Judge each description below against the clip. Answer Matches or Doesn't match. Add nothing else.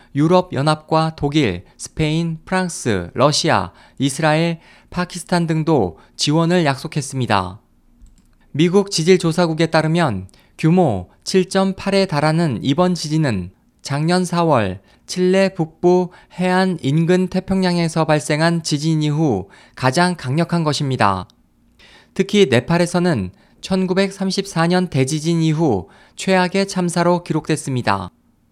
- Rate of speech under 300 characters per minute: Matches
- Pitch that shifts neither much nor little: Matches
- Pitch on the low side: Doesn't match